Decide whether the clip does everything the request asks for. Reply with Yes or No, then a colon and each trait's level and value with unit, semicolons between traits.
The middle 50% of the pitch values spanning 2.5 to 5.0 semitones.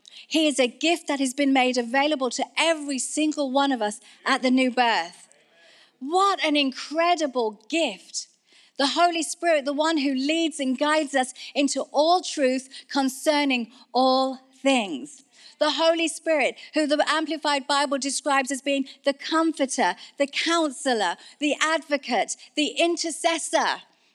Yes: average, 3.1 semitones